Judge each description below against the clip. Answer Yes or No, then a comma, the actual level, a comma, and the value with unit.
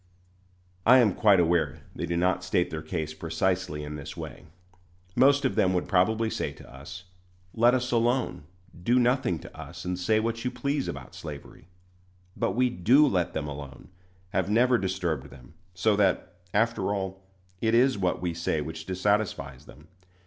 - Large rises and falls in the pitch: Yes, wide, 5.7 semitones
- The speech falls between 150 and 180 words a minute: Yes, average, 170 wpm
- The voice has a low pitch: Yes, very low, 95 Hz